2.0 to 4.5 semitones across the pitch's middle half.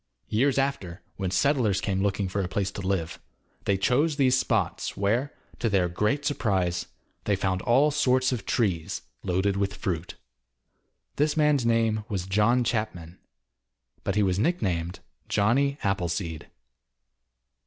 No: average, 5.3 semitones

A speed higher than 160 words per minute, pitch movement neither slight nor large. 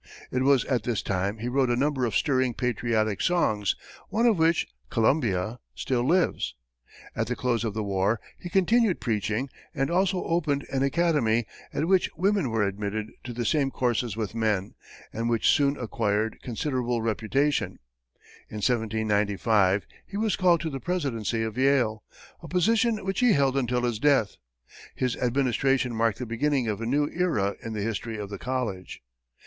Yes: average, 170 wpm; average, 4.9 semitones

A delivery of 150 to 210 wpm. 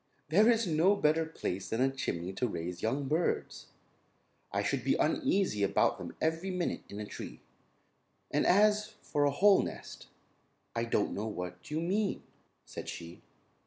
Yes: average, 165 wpm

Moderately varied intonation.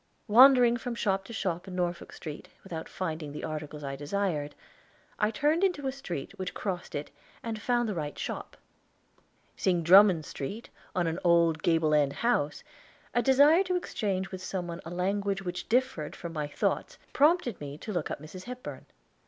No: wide, 6.6 semitones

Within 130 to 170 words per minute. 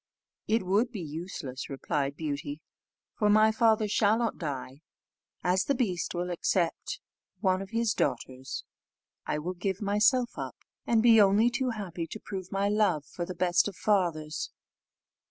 Yes: average, 160 wpm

